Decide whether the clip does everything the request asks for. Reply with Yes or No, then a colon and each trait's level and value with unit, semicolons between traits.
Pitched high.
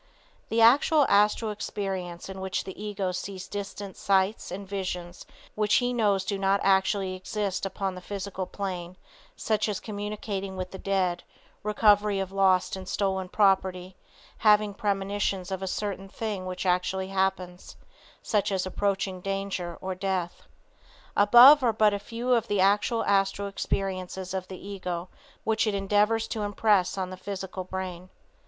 Yes: high, 195 Hz